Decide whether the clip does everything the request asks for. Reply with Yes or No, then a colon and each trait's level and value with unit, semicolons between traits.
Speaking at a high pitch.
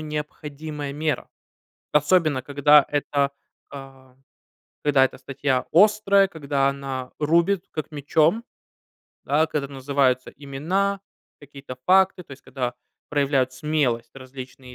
No: medium, 145 Hz